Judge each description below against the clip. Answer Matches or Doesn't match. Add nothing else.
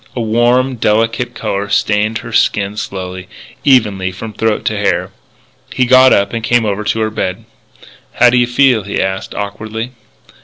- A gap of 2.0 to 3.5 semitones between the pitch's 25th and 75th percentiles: Matches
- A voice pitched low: Matches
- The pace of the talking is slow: Doesn't match